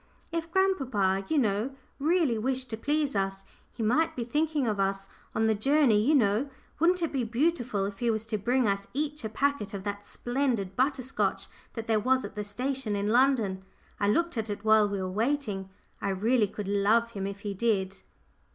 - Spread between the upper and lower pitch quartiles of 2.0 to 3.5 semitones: No, average, 5.2 semitones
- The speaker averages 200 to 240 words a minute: Yes, fast, 205 wpm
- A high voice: Yes, high, 225 Hz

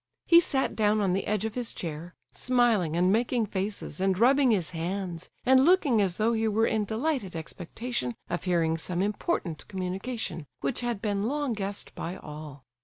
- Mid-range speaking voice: No, high, 205 Hz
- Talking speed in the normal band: Yes, average, 180 wpm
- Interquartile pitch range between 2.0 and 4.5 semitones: No, average, 5.1 semitones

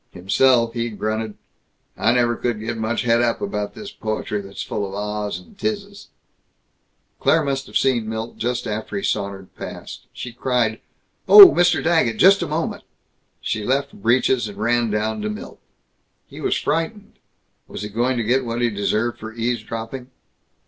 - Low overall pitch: Yes, low, 115 Hz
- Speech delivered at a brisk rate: No, average, 170 wpm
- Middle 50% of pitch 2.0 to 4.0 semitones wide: Yes, average, 3.5 semitones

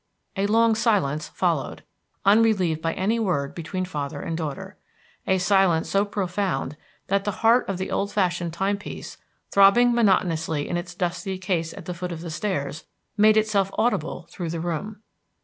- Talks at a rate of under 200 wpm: Yes, average, 165 wpm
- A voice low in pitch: No, medium, 185 Hz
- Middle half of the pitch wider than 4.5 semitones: No, average, 3.7 semitones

